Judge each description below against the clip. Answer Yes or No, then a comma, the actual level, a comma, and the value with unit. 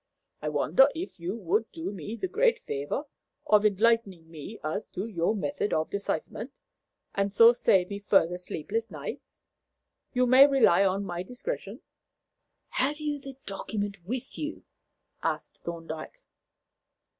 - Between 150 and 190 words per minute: No, average, 140 wpm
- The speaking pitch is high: Yes, high, 205 Hz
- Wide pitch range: Yes, wide, 6.1 semitones